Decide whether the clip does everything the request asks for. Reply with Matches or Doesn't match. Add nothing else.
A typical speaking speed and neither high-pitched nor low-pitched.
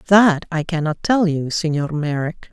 Matches